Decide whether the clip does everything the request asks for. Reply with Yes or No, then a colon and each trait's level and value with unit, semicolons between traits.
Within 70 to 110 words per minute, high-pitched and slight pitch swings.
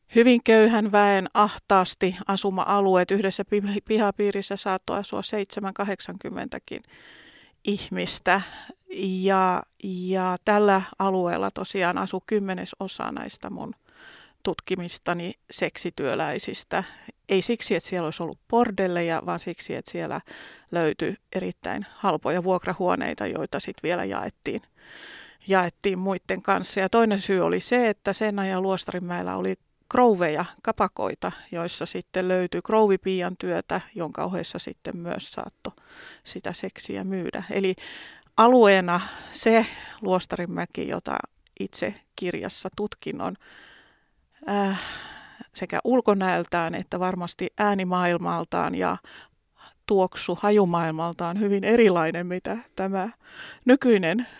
Yes: average, 100 wpm; high, 195 Hz; narrow, 2.3 semitones